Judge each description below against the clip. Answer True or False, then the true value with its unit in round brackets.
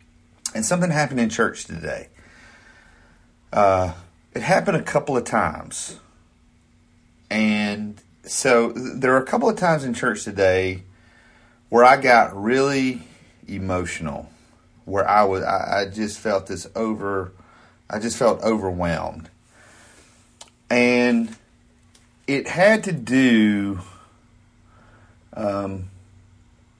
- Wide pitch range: False (4.3 semitones)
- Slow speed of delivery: True (110 wpm)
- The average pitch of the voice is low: True (105 Hz)